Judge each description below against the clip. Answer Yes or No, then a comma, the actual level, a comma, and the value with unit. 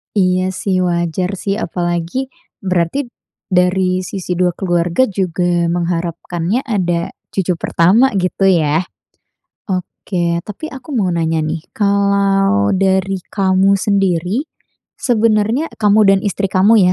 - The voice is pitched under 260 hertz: Yes, medium, 185 Hz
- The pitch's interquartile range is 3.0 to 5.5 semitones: No, narrow, 2.5 semitones